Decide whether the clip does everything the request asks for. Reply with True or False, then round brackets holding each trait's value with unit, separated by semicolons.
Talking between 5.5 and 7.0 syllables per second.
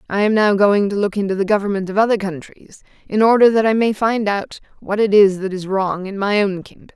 True (5.7 syllables/s)